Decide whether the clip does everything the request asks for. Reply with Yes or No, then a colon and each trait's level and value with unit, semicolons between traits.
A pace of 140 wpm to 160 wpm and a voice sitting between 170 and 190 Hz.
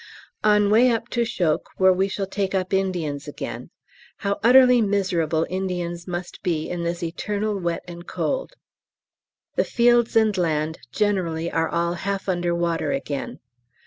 Yes: average, 150 wpm; medium, 185 Hz